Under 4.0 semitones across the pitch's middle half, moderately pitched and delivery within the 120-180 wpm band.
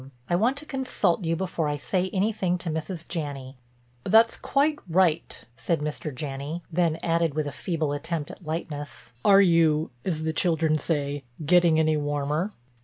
Yes: average, 3.3 semitones; medium, 165 Hz; average, 165 wpm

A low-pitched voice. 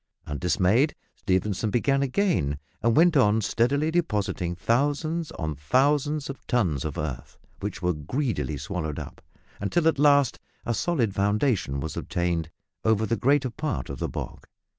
Yes: low, 115 Hz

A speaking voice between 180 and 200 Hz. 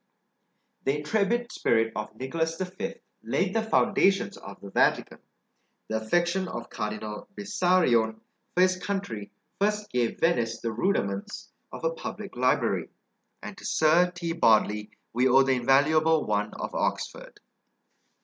No: medium, 150 Hz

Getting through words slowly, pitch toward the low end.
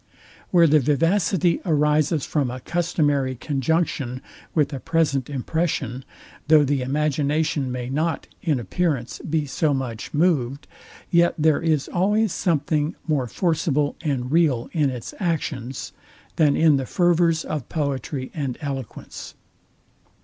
No: slow, 125 wpm; medium, 150 Hz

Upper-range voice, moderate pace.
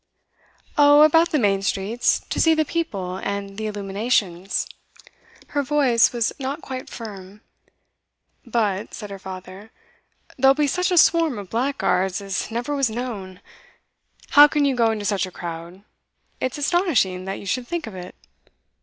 Yes: high, 225 Hz; average, 155 wpm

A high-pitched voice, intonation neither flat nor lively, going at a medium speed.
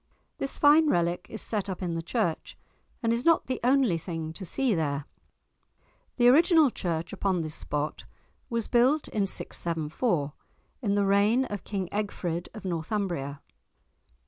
No: high, 200 Hz; wide, 6.3 semitones; average, 150 wpm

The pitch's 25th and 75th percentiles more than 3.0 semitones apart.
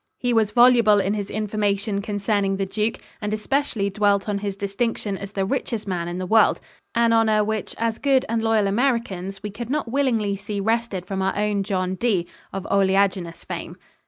No: narrow, 2.4 semitones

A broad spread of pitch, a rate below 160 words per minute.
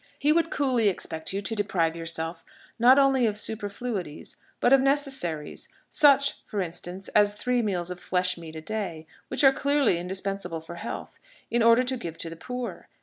No: wide, 6.6 semitones; average, 180 wpm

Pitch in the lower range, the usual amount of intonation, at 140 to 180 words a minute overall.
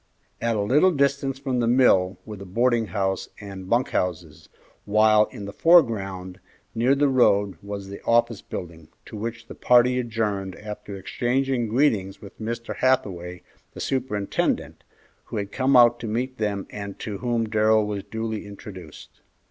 Yes: low, 110 Hz; average, 3.7 semitones; average, 160 wpm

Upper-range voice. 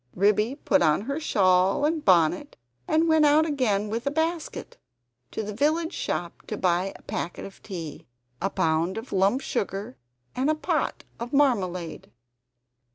Yes: high, 215 Hz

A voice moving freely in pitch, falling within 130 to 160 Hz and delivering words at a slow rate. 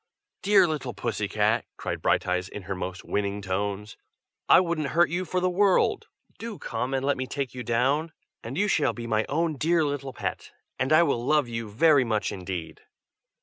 No: wide, 7.2 semitones; low, 135 Hz; average, 190 wpm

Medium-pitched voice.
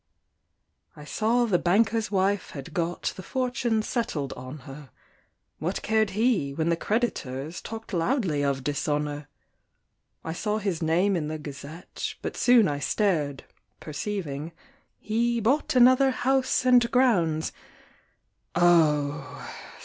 Yes: medium, 180 Hz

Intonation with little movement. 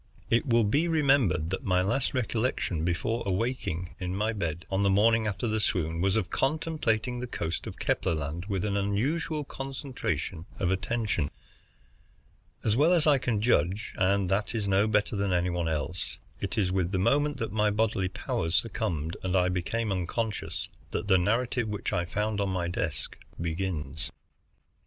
No: average, 4.3 semitones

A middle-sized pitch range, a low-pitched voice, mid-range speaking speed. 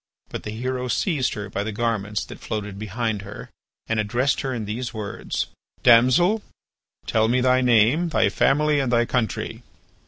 Yes: average, 3.2 semitones; low, 120 Hz; average, 165 wpm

